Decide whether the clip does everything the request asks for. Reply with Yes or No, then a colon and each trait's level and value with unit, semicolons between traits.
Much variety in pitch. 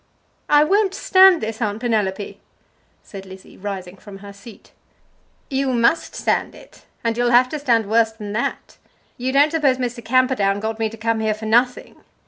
No: average, 3.6 semitones